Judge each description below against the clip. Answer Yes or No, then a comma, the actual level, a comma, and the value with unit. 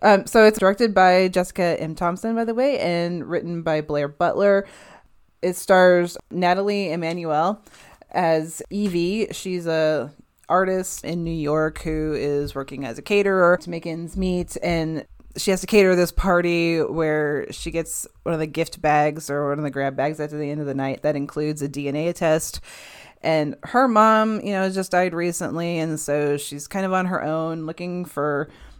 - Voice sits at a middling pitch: Yes, medium, 170 Hz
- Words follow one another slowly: No, average, 185 wpm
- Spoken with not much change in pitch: No, average, 3.6 semitones